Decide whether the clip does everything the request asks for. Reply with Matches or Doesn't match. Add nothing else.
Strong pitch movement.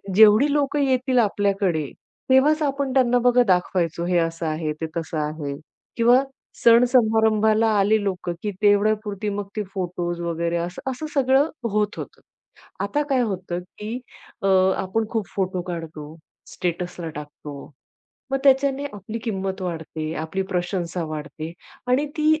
Matches